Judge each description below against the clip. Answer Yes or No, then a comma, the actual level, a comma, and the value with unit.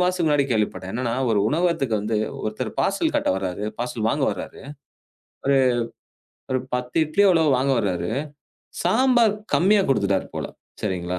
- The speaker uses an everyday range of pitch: No, wide, 7.8 semitones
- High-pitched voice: No, low, 125 Hz